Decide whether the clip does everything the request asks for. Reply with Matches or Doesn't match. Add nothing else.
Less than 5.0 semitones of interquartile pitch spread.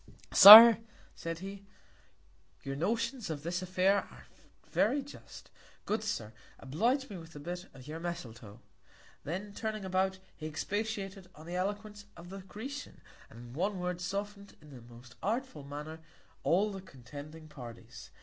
Doesn't match